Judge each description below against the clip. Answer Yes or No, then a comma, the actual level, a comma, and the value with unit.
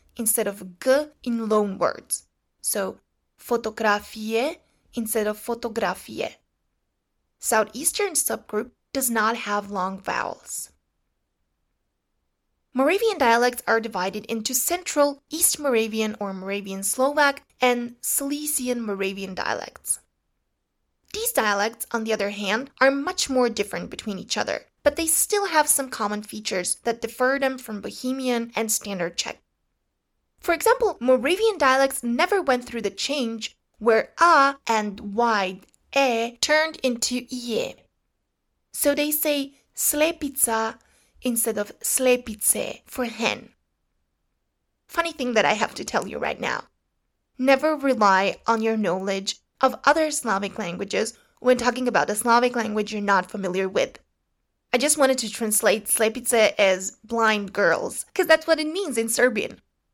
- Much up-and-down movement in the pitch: No, average, 4.5 semitones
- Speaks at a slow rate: Yes, slow, 130 wpm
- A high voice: Yes, high, 240 Hz